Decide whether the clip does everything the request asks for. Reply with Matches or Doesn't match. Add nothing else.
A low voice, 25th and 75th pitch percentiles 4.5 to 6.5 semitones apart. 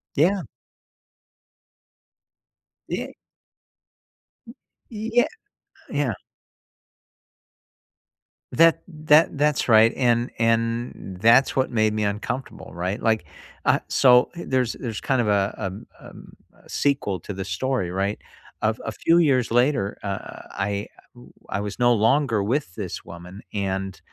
Matches